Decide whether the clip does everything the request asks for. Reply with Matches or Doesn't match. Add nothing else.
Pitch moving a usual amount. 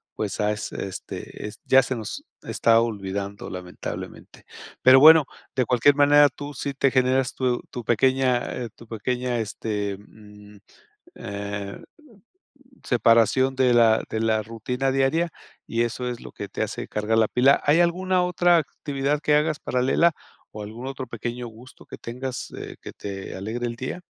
Matches